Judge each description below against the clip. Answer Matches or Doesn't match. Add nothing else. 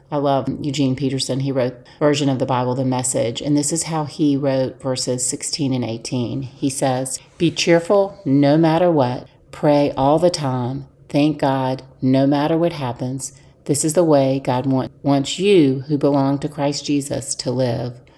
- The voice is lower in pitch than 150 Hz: Matches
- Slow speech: Doesn't match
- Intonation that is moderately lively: Doesn't match